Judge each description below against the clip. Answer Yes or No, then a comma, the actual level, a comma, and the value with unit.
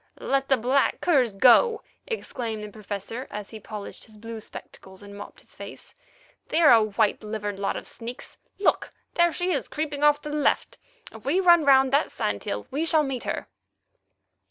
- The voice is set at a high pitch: Yes, high, 245 Hz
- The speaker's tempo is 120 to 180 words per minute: No, average, 190 wpm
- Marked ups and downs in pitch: Yes, wide, 5.9 semitones